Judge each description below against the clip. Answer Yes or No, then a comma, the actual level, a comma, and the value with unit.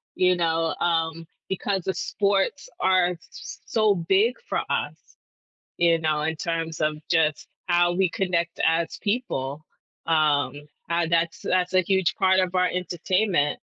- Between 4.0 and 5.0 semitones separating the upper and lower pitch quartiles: No, narrow, 2.5 semitones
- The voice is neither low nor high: Yes, medium, 175 Hz